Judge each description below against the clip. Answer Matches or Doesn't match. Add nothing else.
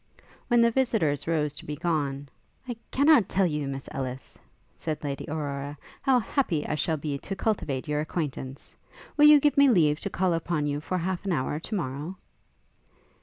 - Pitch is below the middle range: Doesn't match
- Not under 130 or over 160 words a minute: Doesn't match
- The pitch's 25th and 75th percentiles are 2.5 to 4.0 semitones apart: Doesn't match